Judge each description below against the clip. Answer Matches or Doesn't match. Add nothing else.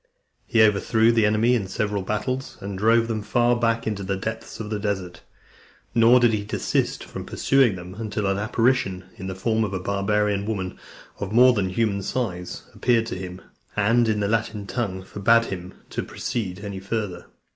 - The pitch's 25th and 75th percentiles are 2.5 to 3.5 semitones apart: Matches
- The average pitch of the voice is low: Matches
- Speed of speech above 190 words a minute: Doesn't match